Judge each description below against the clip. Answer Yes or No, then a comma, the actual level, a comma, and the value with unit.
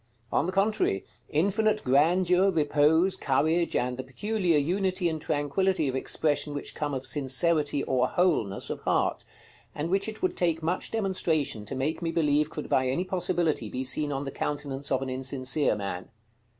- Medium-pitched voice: Yes, medium, 150 Hz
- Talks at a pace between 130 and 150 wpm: No, average, 170 wpm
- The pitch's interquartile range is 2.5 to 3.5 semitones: No, average, 4.9 semitones